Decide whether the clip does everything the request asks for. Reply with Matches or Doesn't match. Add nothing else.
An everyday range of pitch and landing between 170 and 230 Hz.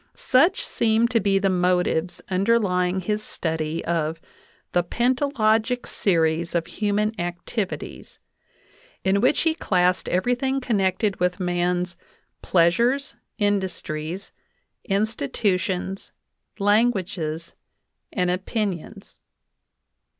Matches